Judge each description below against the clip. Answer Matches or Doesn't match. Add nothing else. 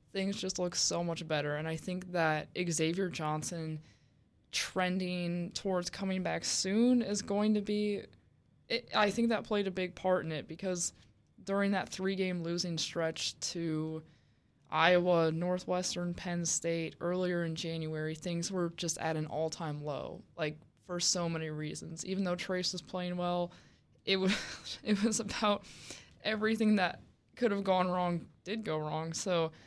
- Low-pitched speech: Doesn't match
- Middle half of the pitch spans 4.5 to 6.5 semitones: Doesn't match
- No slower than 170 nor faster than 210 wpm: Doesn't match